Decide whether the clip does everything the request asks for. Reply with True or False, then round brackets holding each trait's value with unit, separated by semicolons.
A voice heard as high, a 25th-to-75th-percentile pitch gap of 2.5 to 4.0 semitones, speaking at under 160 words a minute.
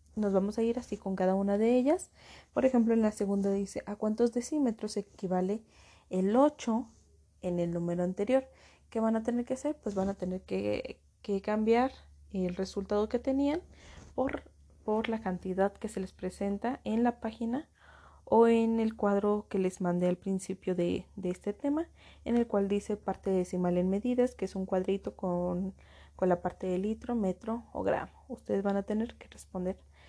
False (205 Hz; 3.6 semitones; 185 wpm)